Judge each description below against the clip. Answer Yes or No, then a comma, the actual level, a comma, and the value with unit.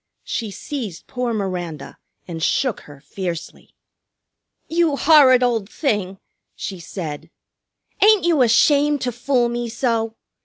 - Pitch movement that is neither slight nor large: No, wide, 6.4 semitones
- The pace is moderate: No, slow, 120 wpm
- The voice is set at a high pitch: Yes, high, 235 Hz